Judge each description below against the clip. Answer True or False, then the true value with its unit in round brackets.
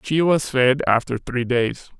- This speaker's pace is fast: False (180 wpm)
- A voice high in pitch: False (130 Hz)